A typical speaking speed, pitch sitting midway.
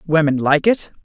Yes: average, 175 wpm; medium, 160 Hz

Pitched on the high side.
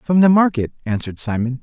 No: medium, 140 Hz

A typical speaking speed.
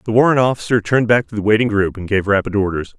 No: fast, 260 wpm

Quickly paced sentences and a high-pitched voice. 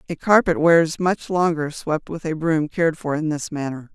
No: fast, 215 wpm; medium, 160 Hz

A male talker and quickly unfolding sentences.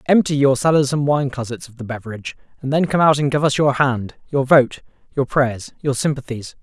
Yes: male; fast, 215 wpm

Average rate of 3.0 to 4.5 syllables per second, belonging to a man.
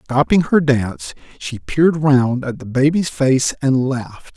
Yes: 4.2 syllables/s; male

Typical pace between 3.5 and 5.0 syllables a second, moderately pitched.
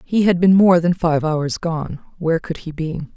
Yes: 4.6 syllables/s; medium, 165 Hz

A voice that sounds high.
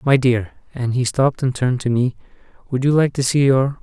No: low, 130 Hz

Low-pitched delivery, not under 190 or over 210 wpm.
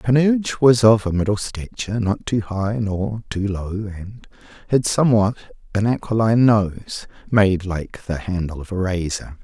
No: low, 105 Hz; average, 160 wpm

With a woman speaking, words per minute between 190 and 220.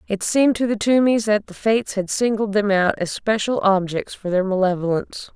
Yes: female; average, 200 wpm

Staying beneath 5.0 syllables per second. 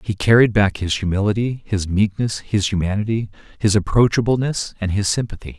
No: 5.5 syllables/s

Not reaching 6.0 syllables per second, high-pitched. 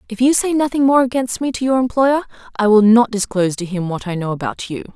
No: 6.1 syllables/s; high, 230 Hz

